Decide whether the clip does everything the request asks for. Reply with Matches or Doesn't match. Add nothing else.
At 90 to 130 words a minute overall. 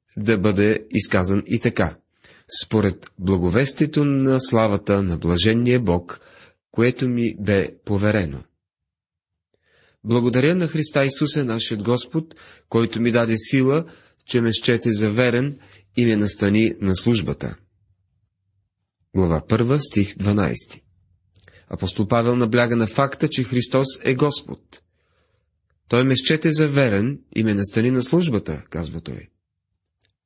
Matches